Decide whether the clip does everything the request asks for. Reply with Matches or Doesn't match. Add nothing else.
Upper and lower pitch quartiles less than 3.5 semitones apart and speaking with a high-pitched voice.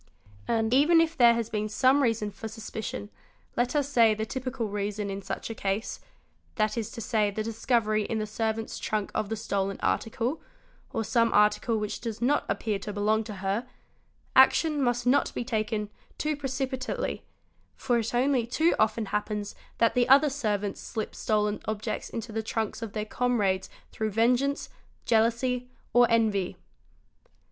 Matches